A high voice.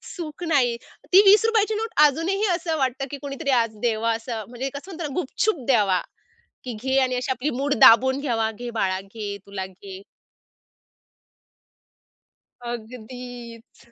Yes: very high, 250 Hz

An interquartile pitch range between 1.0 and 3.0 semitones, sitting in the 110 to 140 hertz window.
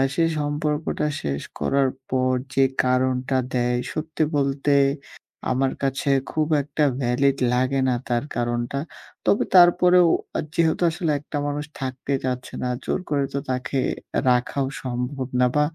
Yes: narrow, 2.6 semitones; low, 135 Hz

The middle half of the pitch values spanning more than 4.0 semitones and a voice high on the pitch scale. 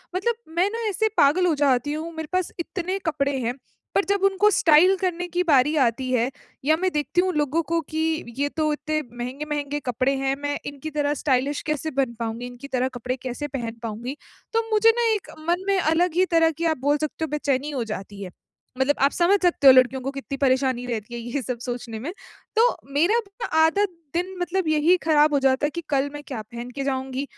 Yes: average, 4.8 semitones; very high, 290 Hz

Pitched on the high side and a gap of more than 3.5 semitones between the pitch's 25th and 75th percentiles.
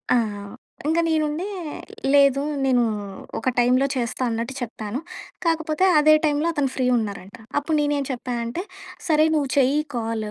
Yes: very high, 275 Hz; average, 3.9 semitones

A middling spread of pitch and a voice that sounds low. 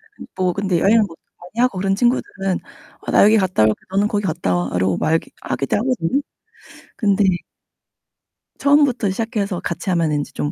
No: average, 4.9 semitones; high, 195 Hz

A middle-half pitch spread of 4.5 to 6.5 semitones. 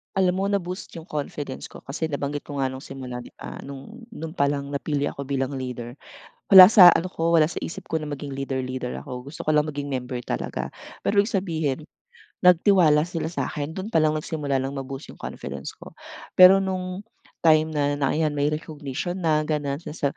No: average, 3.3 semitones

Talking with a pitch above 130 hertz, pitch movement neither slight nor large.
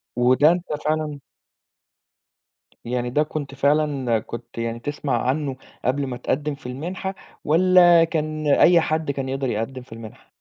Yes: medium, 140 Hz; average, 3.5 semitones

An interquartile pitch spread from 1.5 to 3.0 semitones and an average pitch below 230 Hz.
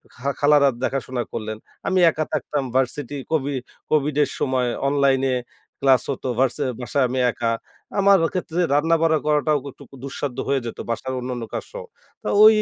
Yes: average, 2.7 semitones; medium, 140 Hz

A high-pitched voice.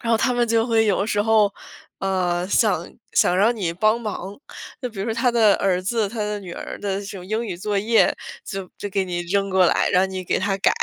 Yes: high, 200 Hz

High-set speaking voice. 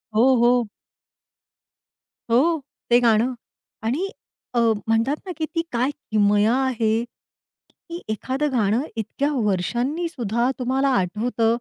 Yes: high, 240 Hz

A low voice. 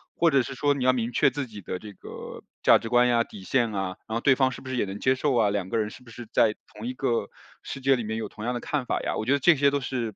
Yes: low, 120 Hz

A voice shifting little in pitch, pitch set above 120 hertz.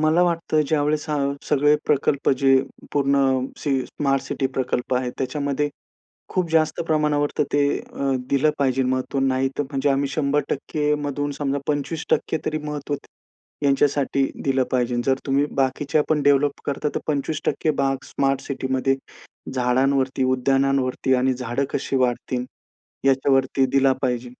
Yes: narrow, 1.8 semitones; medium, 140 Hz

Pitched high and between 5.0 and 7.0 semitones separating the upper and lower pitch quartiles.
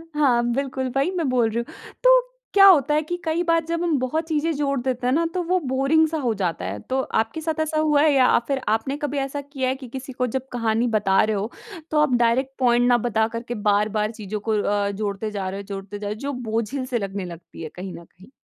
Yes: very high, 255 Hz; wide, 5.5 semitones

